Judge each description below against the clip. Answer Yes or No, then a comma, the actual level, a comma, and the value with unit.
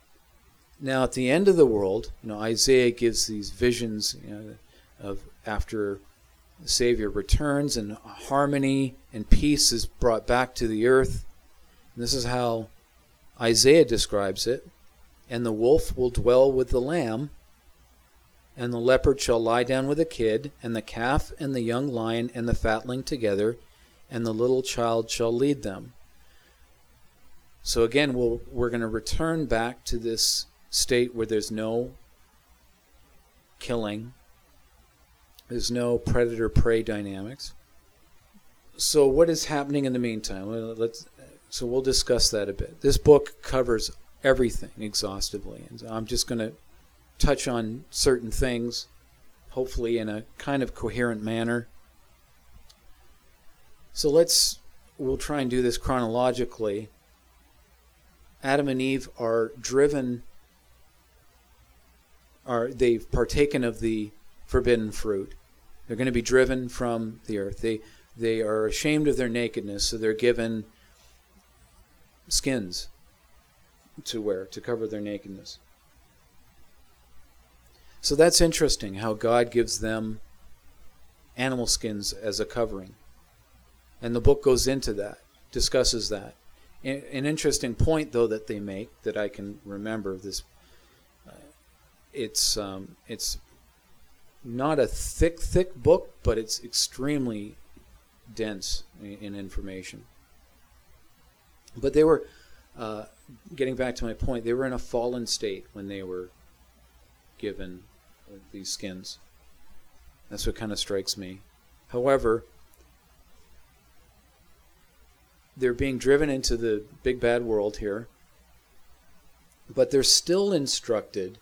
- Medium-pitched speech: No, low, 110 Hz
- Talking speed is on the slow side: Yes, slow, 130 wpm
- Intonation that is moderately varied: No, wide, 7.6 semitones